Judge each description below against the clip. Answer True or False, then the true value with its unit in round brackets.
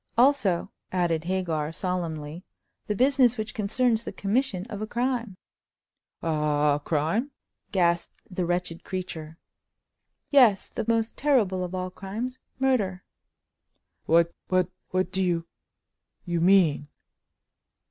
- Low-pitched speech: False (185 Hz)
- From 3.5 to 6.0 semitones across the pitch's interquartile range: True (4.8 semitones)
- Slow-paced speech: True (95 wpm)